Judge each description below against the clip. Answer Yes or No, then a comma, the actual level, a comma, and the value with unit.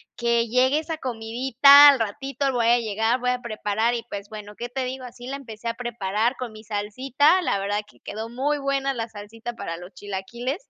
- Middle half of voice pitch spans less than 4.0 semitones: Yes, average, 3.5 semitones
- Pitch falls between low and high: No, high, 235 Hz